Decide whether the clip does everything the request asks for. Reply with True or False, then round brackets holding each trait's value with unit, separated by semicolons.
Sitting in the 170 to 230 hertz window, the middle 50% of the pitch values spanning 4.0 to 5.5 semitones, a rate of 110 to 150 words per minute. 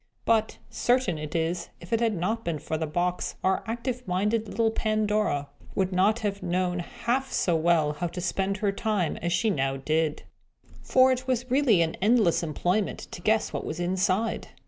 False (190 Hz; 4.6 semitones; 185 wpm)